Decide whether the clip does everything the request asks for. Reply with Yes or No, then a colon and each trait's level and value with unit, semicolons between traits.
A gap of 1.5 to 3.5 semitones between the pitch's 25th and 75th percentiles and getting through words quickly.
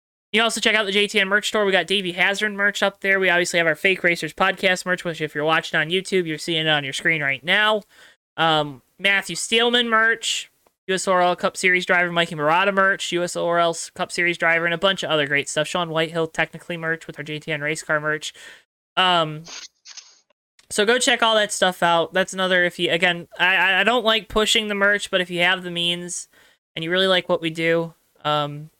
Yes: average, 3.2 semitones; fast, 215 wpm